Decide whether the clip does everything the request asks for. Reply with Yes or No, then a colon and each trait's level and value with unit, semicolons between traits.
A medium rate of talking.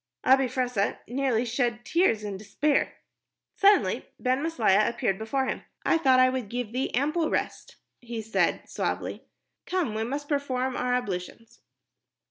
Yes: average, 150 wpm